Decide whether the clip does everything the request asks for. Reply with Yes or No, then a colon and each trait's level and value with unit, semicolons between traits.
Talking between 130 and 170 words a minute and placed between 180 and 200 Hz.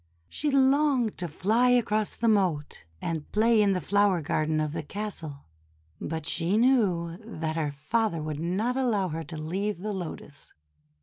Yes: average, 165 wpm; high, 190 Hz